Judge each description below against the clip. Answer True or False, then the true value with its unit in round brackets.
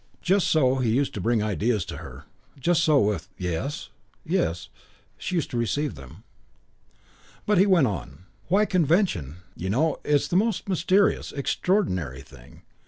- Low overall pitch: True (130 Hz)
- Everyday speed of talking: True (155 wpm)